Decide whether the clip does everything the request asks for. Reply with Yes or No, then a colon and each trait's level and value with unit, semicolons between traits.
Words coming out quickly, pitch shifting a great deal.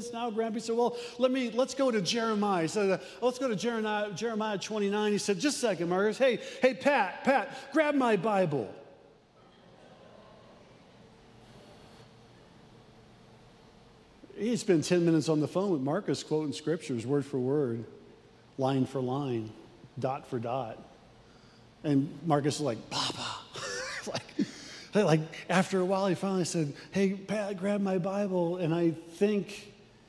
No: average, 145 wpm; wide, 6.3 semitones